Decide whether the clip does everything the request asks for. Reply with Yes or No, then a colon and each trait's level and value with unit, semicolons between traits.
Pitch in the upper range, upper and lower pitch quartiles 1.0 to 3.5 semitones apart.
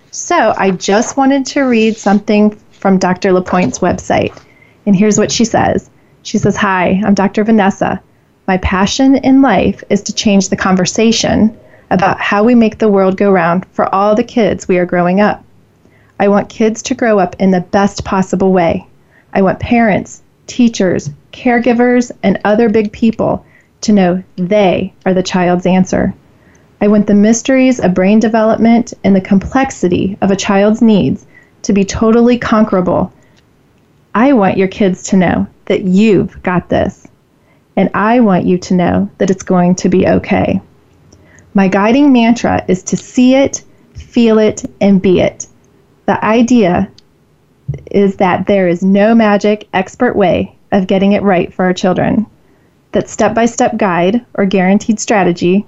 Yes: high, 200 Hz; average, 2.9 semitones